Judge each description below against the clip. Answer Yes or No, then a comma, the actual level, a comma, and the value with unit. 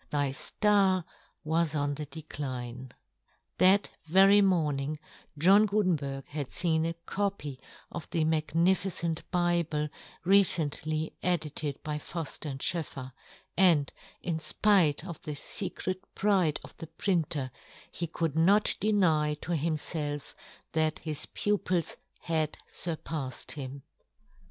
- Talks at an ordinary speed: No, slow, 120 wpm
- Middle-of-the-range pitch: Yes, medium, 160 Hz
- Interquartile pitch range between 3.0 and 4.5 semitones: Yes, average, 3.6 semitones